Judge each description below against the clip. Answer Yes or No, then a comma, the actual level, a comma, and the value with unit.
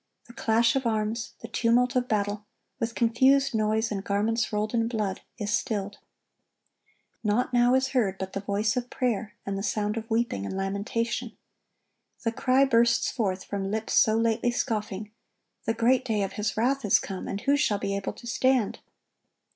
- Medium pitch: No, high, 225 Hz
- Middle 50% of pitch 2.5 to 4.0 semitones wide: Yes, average, 2.8 semitones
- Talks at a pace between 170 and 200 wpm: Yes, average, 180 wpm